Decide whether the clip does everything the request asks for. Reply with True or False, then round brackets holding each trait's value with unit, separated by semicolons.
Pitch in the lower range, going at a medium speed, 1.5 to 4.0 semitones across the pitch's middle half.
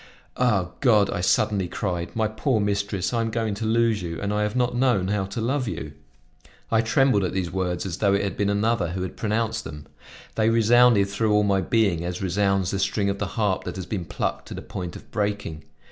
False (100 Hz; 225 wpm; 3.0 semitones)